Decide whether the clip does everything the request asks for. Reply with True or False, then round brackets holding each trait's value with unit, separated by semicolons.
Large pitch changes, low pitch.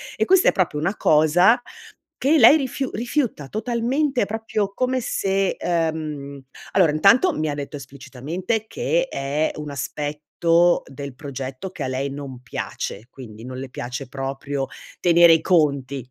False (7.2 semitones; 155 Hz)